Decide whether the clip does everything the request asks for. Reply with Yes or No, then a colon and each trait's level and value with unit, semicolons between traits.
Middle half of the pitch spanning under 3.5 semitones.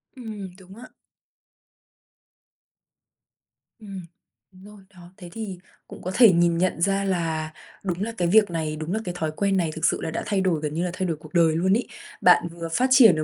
Yes: average, 3.1 semitones